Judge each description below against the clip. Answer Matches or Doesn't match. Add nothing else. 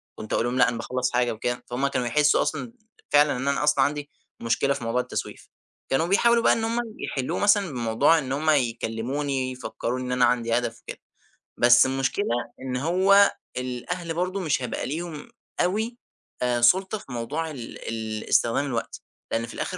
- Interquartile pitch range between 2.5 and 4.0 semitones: Doesn't match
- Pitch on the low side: Matches